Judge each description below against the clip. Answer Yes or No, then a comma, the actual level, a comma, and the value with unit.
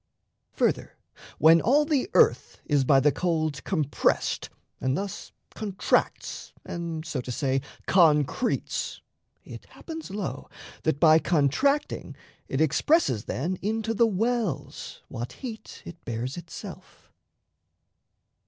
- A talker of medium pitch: Yes, medium, 170 Hz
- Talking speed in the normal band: No, slow, 115 wpm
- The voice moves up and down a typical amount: No, wide, 7.5 semitones